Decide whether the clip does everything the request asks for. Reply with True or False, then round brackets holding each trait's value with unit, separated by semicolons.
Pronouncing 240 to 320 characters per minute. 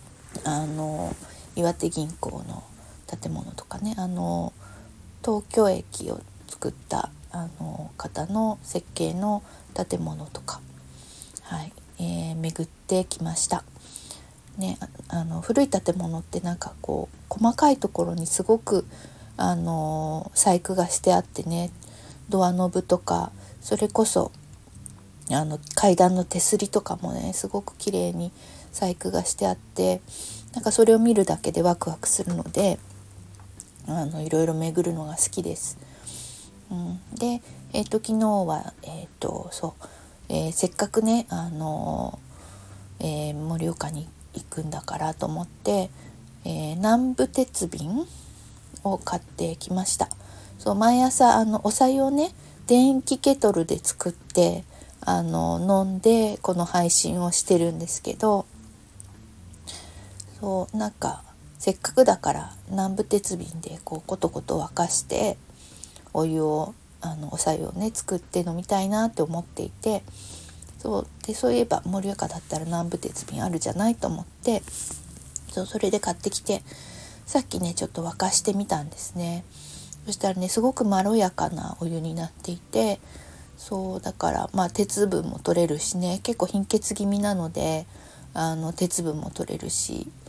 True (265 characters per minute)